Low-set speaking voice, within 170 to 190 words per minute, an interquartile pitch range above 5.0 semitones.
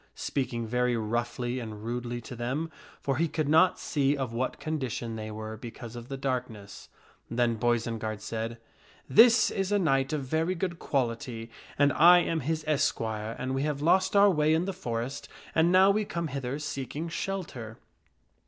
Yes: low, 130 Hz; average, 175 wpm; wide, 5.4 semitones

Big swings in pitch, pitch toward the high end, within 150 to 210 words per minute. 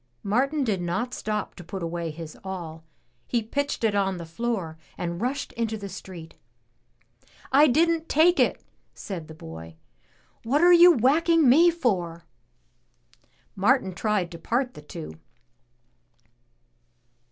No: wide, 7.8 semitones; high, 205 Hz; average, 140 wpm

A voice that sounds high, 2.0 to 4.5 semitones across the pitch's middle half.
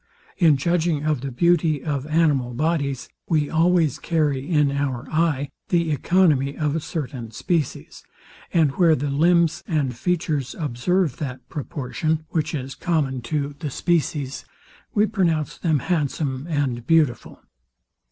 No: medium, 150 Hz; average, 3.2 semitones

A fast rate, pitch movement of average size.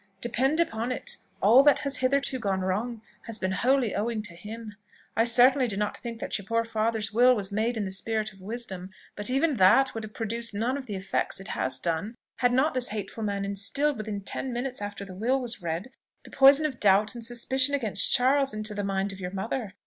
Yes: fast, 220 wpm; average, 4.0 semitones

